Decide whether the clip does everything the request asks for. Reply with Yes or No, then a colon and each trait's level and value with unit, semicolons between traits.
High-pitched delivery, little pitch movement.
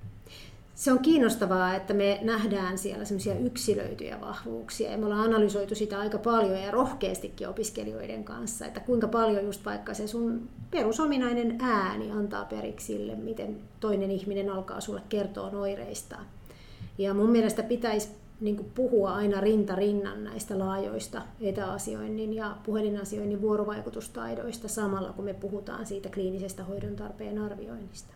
Yes: high, 205 Hz; narrow, 2.3 semitones